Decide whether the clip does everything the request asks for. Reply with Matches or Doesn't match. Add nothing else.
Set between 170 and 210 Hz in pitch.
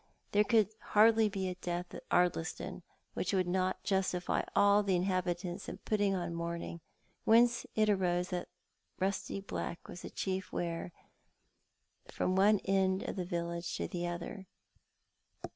Matches